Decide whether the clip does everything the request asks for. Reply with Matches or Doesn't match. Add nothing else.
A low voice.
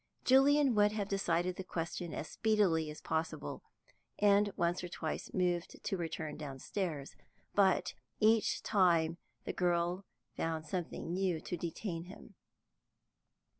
Doesn't match